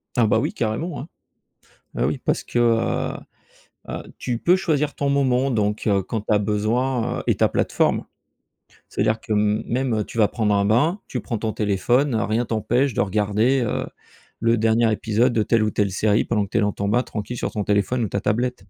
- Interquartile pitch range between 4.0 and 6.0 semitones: No, average, 2.8 semitones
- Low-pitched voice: Yes, low, 115 Hz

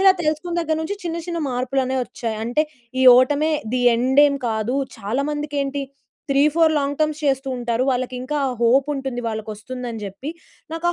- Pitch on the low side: No, very high, 270 Hz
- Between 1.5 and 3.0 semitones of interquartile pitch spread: No, average, 3.6 semitones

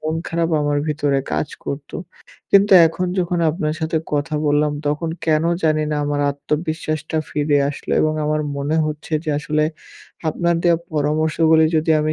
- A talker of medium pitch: Yes, medium, 155 Hz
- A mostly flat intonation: Yes, narrow, 1.5 semitones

